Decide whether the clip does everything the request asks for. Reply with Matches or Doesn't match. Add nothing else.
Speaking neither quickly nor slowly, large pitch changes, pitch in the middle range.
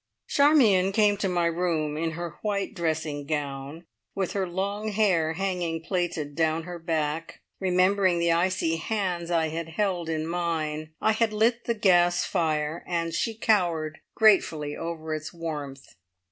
Doesn't match